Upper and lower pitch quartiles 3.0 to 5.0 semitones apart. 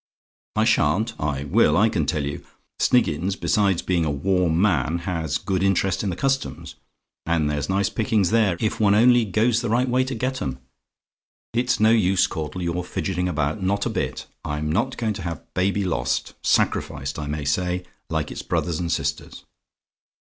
No: wide, 5.5 semitones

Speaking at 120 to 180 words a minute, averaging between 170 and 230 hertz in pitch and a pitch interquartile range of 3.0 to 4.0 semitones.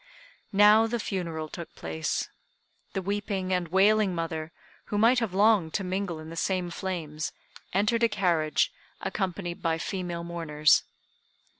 Yes: average, 140 wpm; medium, 185 Hz; average, 3.7 semitones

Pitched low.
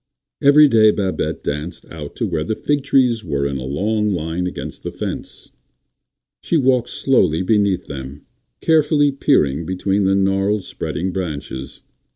Yes: very low, 95 Hz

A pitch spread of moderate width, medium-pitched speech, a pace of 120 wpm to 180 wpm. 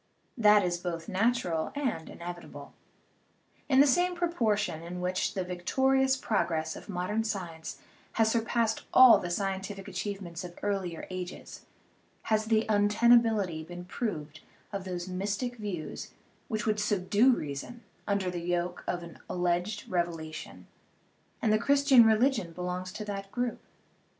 No: average, 4.2 semitones; high, 195 Hz; average, 140 wpm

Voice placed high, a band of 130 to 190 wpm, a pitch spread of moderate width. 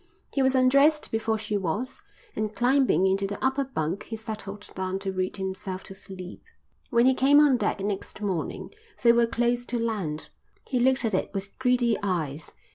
Yes: high, 220 Hz; average, 185 wpm; average, 4.7 semitones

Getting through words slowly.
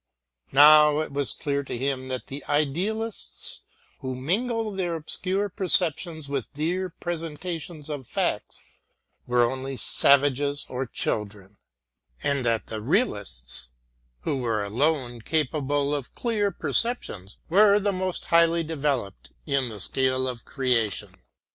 Yes: slow, 125 wpm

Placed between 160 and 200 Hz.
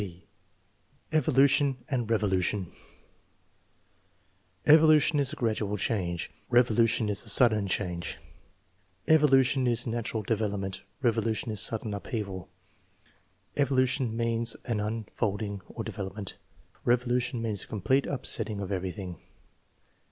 No: low, 110 Hz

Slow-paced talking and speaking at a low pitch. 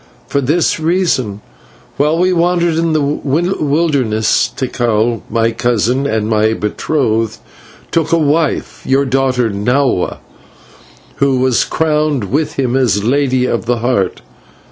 Yes: slow, 125 wpm; low, 130 Hz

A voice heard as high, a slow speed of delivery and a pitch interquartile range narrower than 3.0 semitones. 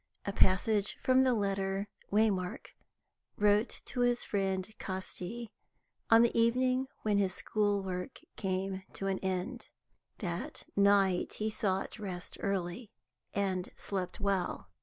Yes: high, 200 Hz; slow, 125 wpm; narrow, 2.5 semitones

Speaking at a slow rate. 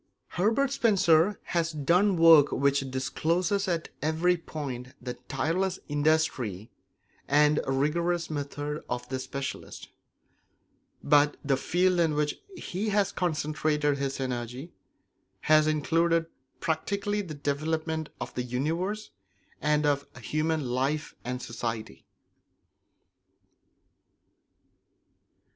Yes: slow, 100 wpm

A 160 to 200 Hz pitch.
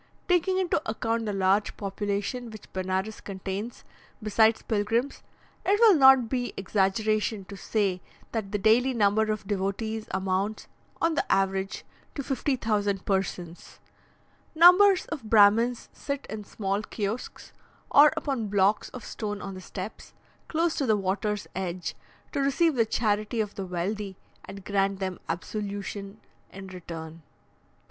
No: high, 210 Hz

